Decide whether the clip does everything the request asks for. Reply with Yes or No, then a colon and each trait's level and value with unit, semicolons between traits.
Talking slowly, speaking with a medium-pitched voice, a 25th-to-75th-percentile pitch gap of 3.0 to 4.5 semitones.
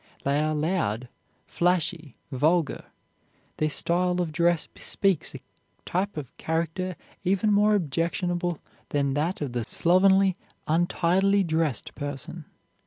Yes: slow, 115 wpm; medium, 170 Hz; average, 3.3 semitones